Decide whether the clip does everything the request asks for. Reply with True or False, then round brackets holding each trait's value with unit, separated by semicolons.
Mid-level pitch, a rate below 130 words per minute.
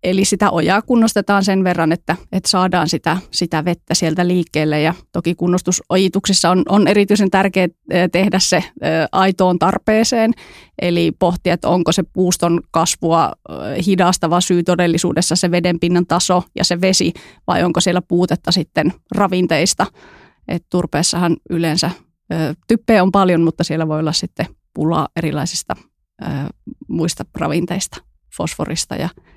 False (180 Hz; 135 wpm)